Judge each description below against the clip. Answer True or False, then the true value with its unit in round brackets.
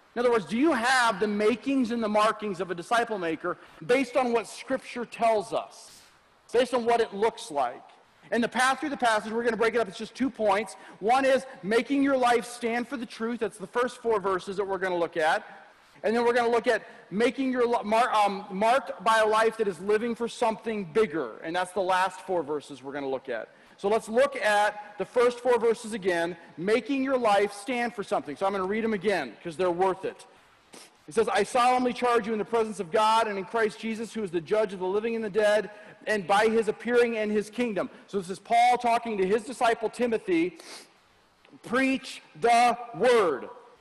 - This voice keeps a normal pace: False (225 wpm)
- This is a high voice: True (225 Hz)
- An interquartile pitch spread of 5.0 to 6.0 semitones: False (3.1 semitones)